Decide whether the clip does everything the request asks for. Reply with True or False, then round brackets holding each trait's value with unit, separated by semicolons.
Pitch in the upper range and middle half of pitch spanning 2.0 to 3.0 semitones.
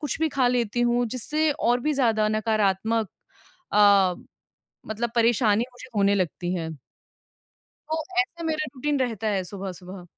False (225 Hz; 4.2 semitones)